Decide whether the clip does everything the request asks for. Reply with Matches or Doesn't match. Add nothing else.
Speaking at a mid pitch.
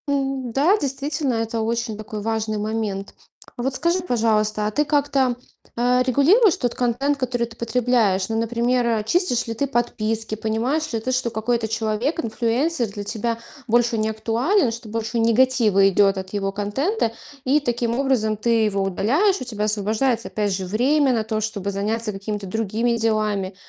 Doesn't match